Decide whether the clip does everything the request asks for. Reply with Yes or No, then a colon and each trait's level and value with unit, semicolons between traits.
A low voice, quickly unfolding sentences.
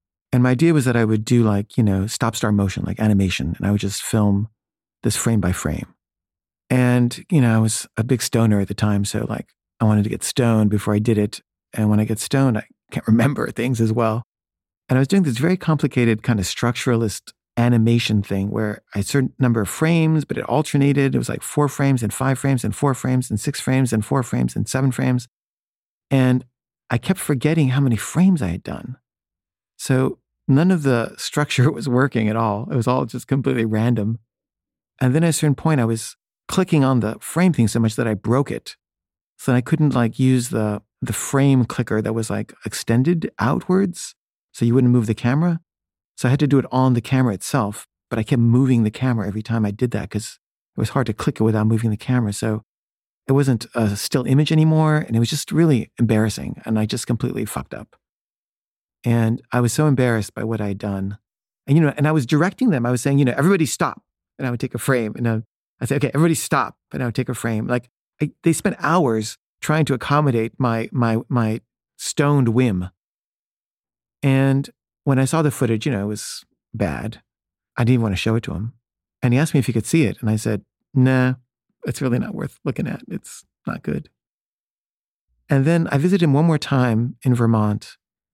Yes: low, 120 Hz; fast, 220 wpm